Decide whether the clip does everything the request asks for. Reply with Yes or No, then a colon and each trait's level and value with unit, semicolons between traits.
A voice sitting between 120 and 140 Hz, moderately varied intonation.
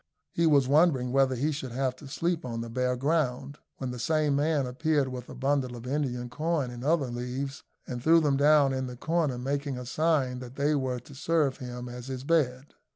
Yes: low, 135 Hz; average, 3.1 semitones